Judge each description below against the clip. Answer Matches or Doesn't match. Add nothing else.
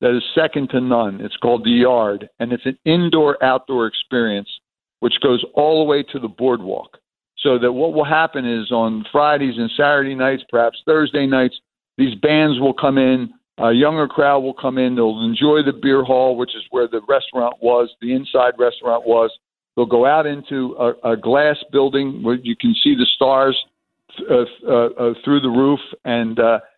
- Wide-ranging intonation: Doesn't match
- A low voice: Matches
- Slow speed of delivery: Doesn't match